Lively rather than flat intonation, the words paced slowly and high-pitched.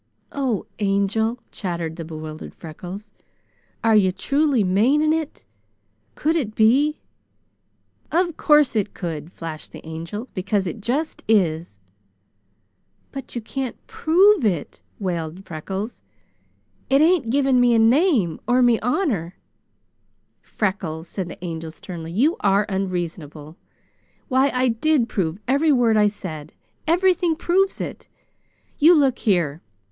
Yes: wide, 7.9 semitones; slow, 125 wpm; high, 215 Hz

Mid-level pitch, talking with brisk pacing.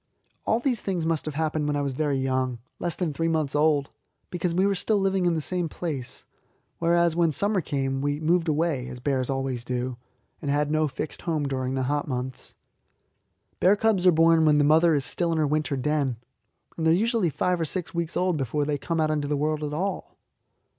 Yes: medium, 155 Hz; fast, 220 wpm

